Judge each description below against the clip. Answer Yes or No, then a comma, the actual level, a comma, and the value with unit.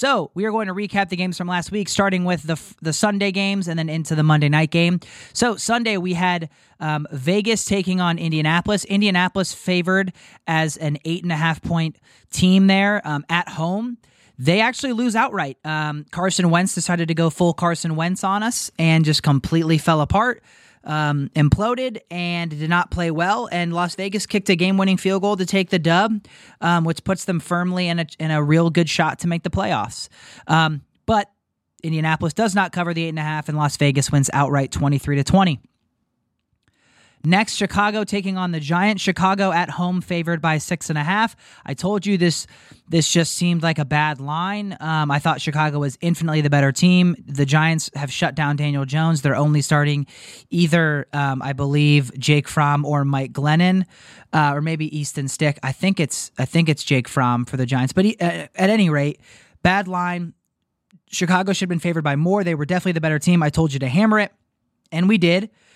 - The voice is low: No, medium, 170 Hz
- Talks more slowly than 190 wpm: No, fast, 205 wpm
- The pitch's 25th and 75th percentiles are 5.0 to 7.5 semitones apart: No, average, 3.8 semitones